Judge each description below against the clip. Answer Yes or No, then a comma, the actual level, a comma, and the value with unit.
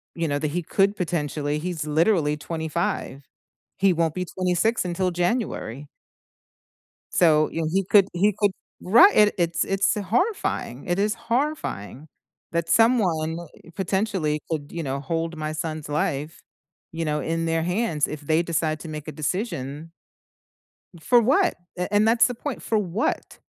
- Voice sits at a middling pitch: Yes, medium, 170 Hz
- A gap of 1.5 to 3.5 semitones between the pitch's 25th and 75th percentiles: No, average, 4.6 semitones